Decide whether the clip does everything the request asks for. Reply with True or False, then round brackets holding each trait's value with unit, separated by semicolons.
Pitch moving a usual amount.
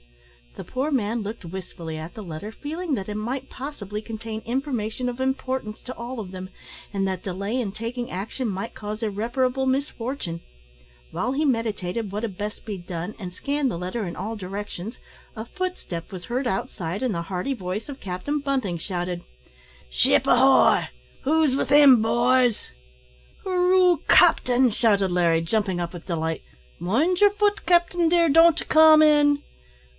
False (6.3 semitones)